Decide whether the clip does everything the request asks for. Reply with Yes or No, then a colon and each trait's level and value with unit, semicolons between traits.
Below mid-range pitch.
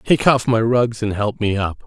Yes: low, 115 Hz